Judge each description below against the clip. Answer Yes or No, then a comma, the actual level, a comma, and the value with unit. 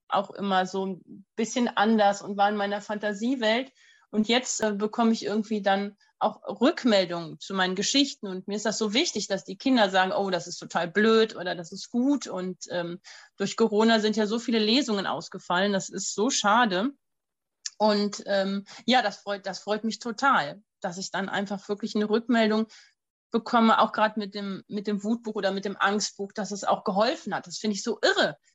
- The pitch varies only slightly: Yes, narrow, 2.2 semitones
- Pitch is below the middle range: No, high, 210 Hz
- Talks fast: Yes, fast, 200 wpm